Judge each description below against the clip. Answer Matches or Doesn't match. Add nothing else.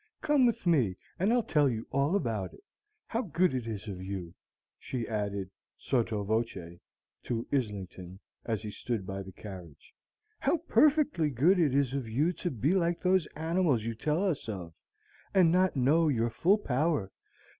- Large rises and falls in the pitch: Matches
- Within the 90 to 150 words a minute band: Doesn't match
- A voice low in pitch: Matches